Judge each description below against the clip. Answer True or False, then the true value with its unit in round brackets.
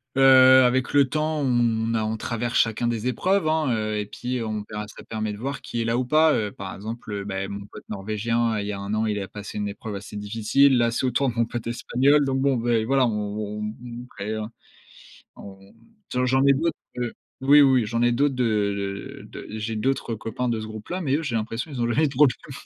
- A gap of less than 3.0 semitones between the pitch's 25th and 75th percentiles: False (3.6 semitones)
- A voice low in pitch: True (115 Hz)